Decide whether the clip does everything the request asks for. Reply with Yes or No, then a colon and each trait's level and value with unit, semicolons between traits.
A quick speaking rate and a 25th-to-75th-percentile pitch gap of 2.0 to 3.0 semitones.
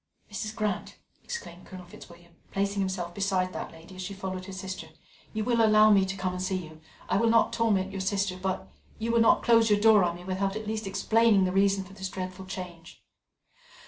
Yes: fast, 210 wpm; narrow, 2.4 semitones